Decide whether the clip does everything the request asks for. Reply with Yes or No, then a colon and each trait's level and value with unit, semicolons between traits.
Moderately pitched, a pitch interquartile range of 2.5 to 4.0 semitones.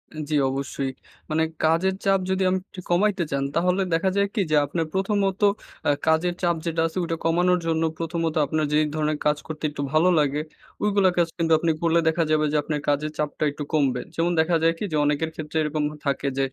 Yes: medium, 160 Hz; average, 2.8 semitones